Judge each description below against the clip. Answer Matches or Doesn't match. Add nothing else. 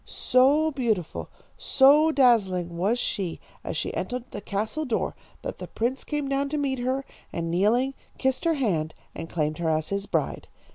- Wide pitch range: Matches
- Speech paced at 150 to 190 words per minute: Matches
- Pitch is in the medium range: Doesn't match